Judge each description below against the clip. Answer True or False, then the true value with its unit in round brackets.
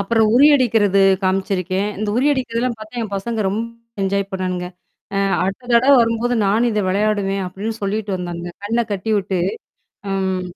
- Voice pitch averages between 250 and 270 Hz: False (205 Hz)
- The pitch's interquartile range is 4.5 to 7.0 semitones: False (3.1 semitones)